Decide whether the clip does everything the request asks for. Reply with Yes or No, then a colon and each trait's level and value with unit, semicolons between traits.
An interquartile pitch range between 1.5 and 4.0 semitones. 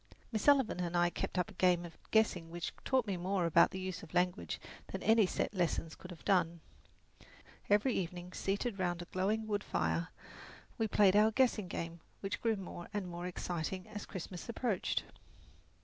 Yes: average, 3.2 semitones